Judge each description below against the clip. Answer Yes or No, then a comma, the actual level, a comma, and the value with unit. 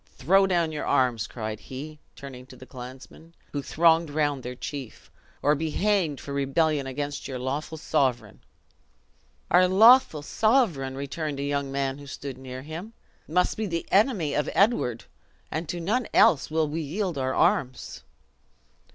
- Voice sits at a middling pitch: Yes, medium, 150 Hz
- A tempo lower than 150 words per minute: No, average, 160 wpm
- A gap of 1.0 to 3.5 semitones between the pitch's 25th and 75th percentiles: No, average, 4.0 semitones